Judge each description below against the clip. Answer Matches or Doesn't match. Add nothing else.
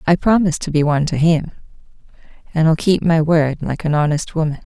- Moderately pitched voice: Matches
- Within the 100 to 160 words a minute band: Doesn't match